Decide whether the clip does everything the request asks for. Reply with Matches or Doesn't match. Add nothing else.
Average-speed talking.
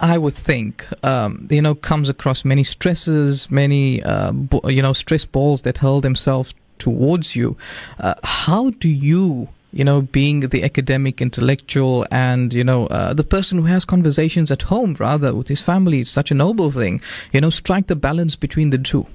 Matches